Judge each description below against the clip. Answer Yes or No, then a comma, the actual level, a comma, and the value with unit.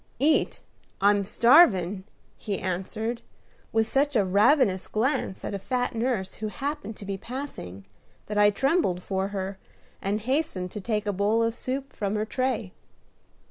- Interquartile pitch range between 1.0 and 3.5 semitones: No, average, 4.7 semitones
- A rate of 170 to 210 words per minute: No, average, 155 wpm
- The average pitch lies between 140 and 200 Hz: No, high, 210 Hz